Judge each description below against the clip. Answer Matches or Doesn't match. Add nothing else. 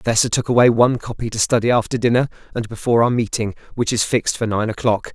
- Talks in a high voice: Doesn't match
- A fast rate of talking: Matches